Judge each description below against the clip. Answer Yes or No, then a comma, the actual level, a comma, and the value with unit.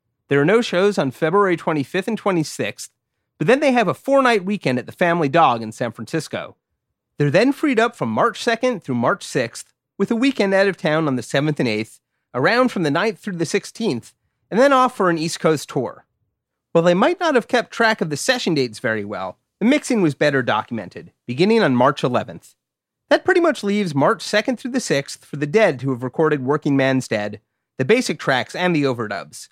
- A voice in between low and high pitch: Yes, medium, 170 Hz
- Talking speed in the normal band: No, fast, 215 wpm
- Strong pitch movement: Yes, wide, 8.8 semitones